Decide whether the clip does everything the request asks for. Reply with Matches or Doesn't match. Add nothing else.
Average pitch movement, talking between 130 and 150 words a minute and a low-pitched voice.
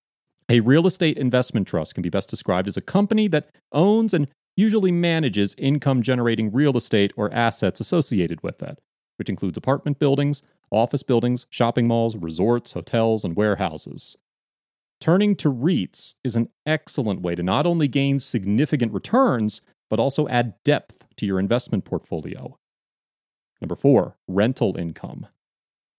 Matches